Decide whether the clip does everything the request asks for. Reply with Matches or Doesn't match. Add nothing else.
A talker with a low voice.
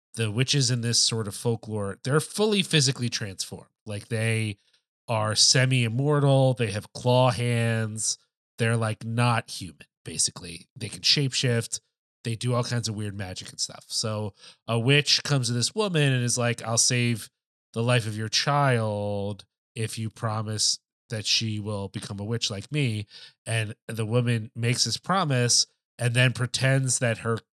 Matches